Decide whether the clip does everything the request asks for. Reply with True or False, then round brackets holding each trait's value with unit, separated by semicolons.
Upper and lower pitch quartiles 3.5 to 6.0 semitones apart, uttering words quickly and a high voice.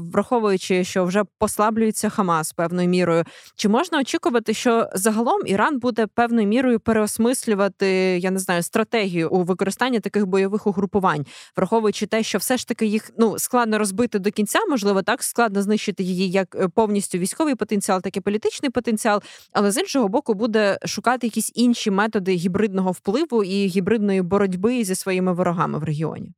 False (3.0 semitones; 160 wpm; 210 Hz)